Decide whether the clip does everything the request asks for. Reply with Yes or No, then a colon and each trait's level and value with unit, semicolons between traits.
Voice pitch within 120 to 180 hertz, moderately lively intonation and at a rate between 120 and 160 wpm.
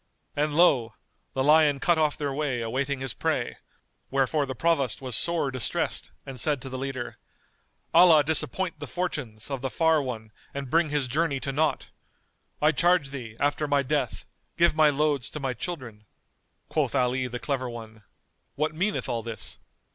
No: medium, 140 Hz; average, 3.4 semitones; average, 170 wpm